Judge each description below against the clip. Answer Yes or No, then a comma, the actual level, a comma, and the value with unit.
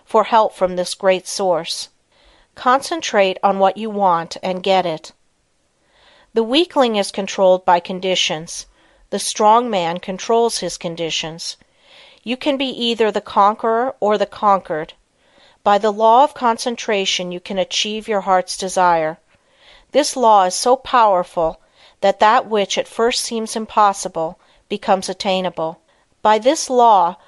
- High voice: Yes, high, 200 Hz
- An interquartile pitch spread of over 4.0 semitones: No, average, 3.7 semitones